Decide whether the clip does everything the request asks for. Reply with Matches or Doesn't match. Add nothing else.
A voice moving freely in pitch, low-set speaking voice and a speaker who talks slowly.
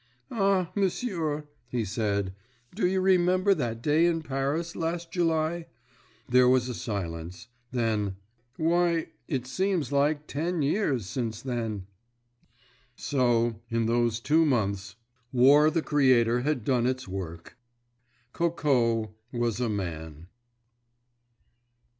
Matches